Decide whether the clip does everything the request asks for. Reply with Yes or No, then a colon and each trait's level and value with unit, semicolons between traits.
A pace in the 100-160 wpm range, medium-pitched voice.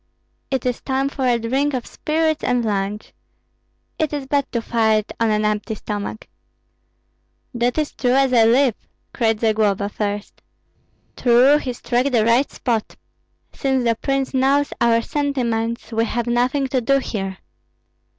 No: average, 155 wpm; high, 240 Hz